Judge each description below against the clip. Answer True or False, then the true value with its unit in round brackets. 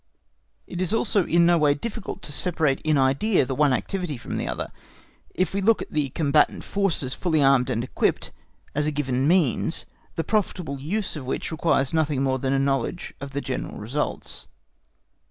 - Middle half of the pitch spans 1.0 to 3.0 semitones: False (4.5 semitones)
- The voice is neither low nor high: True (150 Hz)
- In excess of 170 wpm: True (185 wpm)